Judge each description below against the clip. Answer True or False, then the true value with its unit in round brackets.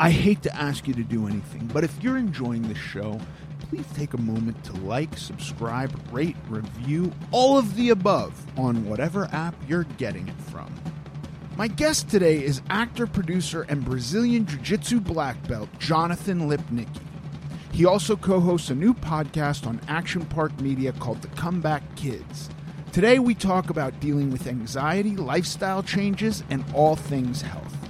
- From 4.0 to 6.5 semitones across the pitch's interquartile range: True (4.8 semitones)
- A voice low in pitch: False (155 Hz)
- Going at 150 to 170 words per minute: True (160 wpm)